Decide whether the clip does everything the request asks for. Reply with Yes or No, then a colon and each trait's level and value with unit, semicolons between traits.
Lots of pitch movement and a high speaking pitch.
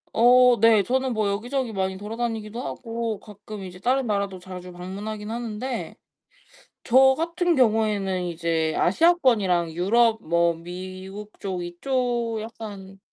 No: average, 4.2 semitones; high, 215 Hz